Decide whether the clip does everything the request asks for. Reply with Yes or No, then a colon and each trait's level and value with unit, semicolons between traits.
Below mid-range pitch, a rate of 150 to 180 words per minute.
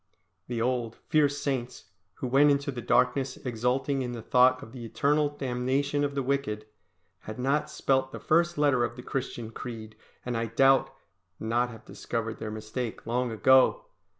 Yes: low, 125 Hz; average, 170 wpm